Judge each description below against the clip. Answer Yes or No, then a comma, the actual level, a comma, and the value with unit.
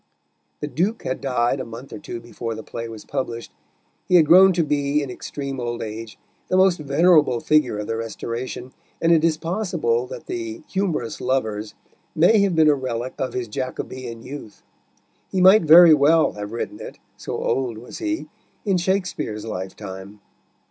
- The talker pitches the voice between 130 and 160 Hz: Yes, low, 135 Hz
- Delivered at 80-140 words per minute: No, average, 175 wpm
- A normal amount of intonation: No, wide, 6.6 semitones